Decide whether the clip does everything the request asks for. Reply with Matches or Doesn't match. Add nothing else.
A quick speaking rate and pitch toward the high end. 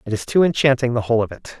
Doesn't match